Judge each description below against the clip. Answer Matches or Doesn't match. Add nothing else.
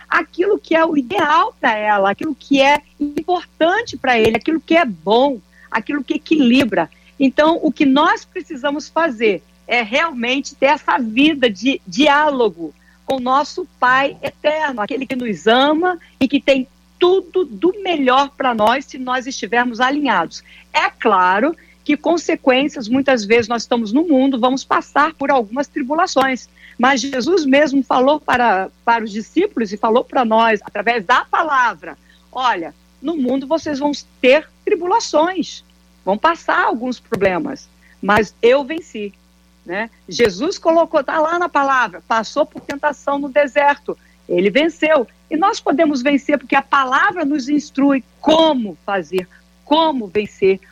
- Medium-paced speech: Matches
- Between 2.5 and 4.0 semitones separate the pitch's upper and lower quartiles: Doesn't match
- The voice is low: Doesn't match